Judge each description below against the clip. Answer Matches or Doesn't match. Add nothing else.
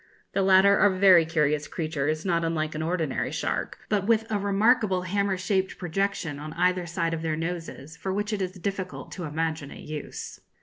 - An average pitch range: Matches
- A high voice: Doesn't match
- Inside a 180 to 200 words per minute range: Matches